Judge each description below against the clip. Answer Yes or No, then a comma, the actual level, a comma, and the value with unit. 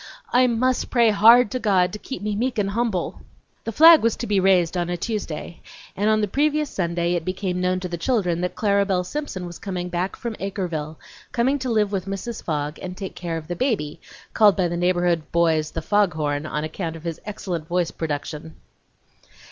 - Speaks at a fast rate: Yes, fast, 210 wpm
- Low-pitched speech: No, medium, 185 Hz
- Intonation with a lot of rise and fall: No, average, 4.0 semitones